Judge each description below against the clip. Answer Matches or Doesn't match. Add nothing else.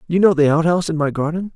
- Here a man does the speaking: Matches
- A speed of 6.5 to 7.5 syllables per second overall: Matches